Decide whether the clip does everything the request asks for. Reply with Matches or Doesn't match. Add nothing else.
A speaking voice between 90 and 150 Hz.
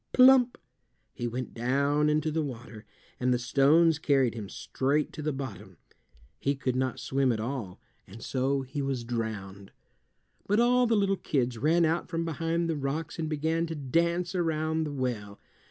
Matches